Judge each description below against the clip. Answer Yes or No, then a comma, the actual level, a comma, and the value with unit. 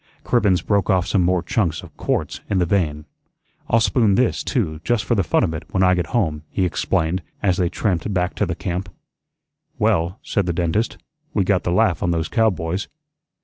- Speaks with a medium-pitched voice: No, very low, 90 Hz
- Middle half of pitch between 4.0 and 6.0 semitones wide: No, average, 3.1 semitones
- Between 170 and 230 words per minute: Yes, average, 200 wpm